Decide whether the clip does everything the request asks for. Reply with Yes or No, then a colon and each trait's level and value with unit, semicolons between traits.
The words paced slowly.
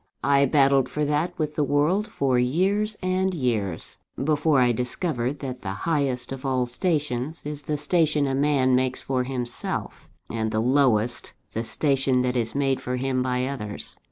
No: average, 170 wpm